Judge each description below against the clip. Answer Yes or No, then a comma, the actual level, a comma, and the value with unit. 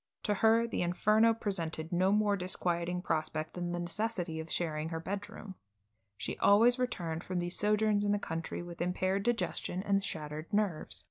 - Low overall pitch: No, medium, 185 Hz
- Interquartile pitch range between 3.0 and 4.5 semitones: Yes, average, 3.6 semitones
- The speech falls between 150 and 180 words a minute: Yes, average, 170 wpm